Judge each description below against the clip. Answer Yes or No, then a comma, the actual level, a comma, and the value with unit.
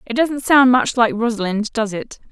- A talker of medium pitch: No, high, 235 Hz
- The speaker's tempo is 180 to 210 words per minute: Yes, fast, 205 wpm